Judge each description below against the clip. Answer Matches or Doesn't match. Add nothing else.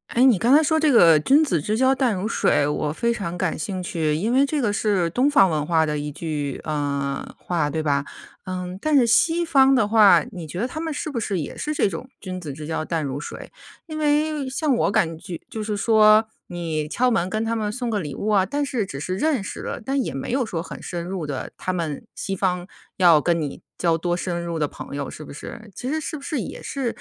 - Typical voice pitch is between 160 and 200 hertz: Matches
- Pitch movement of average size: Doesn't match